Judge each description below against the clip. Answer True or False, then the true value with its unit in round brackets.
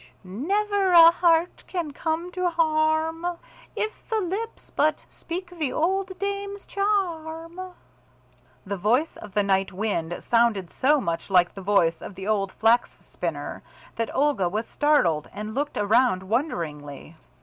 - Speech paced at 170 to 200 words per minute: False (150 wpm)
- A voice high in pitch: True (295 Hz)